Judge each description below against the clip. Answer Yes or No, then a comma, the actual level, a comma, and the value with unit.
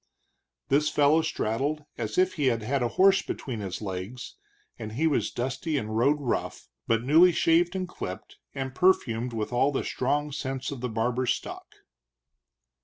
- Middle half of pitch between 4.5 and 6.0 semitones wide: Yes, average, 4.8 semitones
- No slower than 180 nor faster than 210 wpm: No, average, 165 wpm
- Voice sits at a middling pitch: No, low, 130 Hz